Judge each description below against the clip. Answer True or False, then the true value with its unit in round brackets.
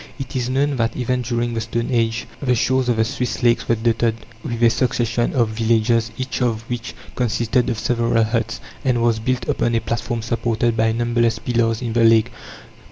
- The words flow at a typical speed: True (195 wpm)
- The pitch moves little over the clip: True (1.3 semitones)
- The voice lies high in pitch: False (115 Hz)